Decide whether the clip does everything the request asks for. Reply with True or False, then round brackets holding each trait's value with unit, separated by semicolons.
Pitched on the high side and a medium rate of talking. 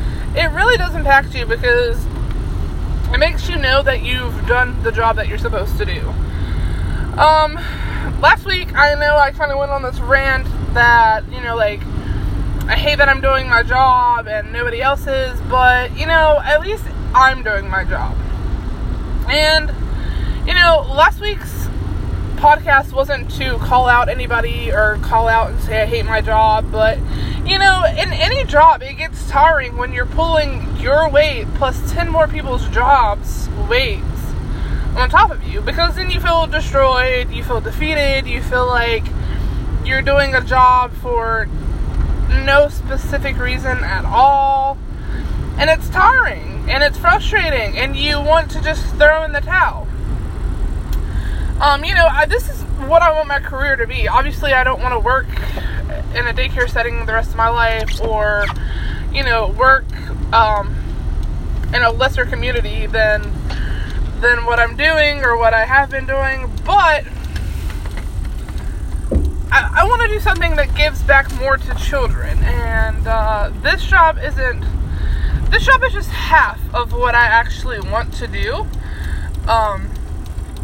True (250 Hz; 160 wpm)